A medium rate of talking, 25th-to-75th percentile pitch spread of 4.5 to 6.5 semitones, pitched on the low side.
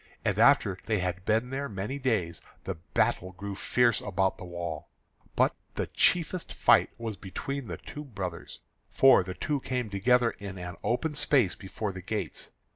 Yes: average, 170 wpm; average, 5.3 semitones; low, 100 Hz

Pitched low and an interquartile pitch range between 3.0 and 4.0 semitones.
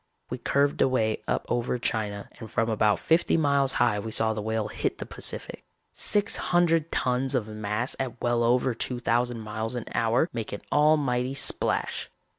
Yes: low, 120 Hz; average, 3.3 semitones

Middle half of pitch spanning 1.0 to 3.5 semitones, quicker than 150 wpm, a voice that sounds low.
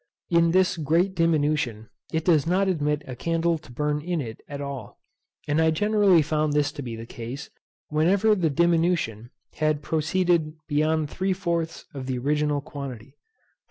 No: average, 3.0 semitones; average, 160 wpm; medium, 155 Hz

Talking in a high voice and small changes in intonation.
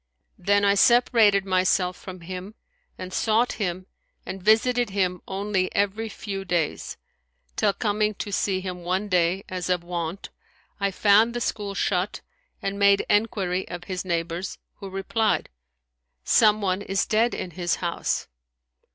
Yes: high, 195 Hz; narrow, 2.3 semitones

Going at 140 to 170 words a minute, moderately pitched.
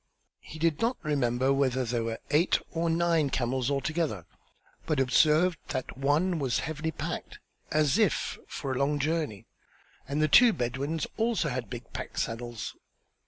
Yes: average, 155 wpm; medium, 145 Hz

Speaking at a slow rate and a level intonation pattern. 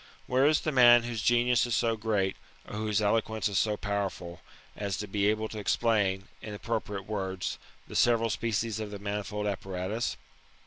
No: average, 180 wpm; narrow, 2.3 semitones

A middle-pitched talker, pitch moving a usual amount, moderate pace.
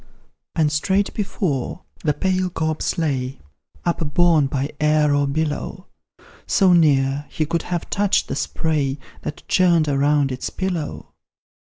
No: medium, 155 Hz; average, 3.4 semitones; slow, 130 wpm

